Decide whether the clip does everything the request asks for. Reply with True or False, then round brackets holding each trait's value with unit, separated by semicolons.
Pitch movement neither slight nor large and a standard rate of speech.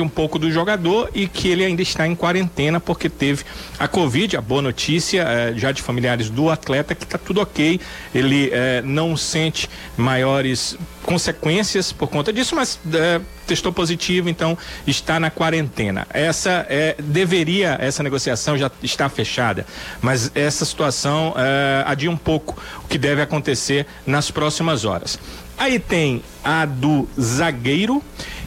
True (3.8 semitones; 150 wpm)